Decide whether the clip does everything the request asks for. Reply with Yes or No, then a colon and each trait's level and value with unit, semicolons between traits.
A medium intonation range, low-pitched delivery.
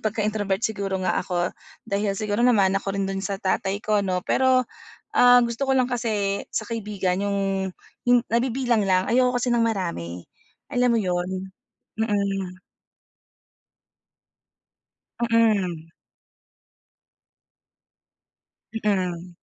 No: average, 3.3 semitones; high, 200 Hz